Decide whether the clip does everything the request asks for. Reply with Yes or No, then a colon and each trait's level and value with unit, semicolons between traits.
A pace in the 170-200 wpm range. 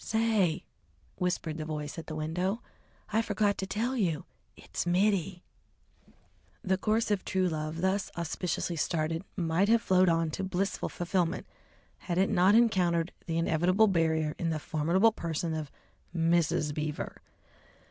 No: average, 145 wpm